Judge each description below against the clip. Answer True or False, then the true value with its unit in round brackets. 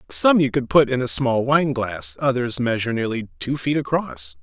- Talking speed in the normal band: True (190 wpm)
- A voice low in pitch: True (125 Hz)